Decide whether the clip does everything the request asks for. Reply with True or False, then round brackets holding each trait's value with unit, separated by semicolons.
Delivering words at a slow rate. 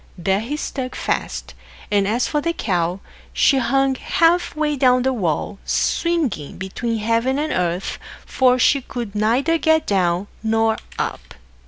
False (150 wpm)